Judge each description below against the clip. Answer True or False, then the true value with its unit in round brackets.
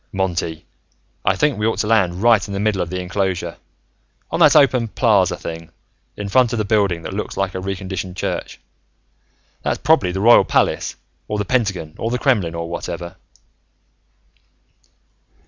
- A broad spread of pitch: False (3.8 semitones)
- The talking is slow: False (165 wpm)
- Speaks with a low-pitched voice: True (95 Hz)